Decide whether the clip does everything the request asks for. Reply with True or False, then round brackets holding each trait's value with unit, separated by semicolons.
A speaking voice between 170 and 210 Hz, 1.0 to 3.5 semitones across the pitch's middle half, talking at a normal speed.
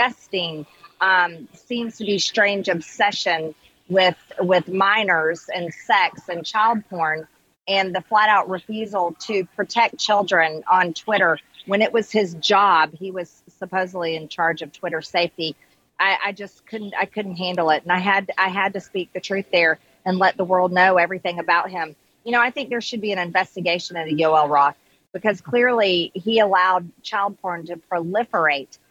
True (185 Hz; 3.1 semitones; 170 wpm)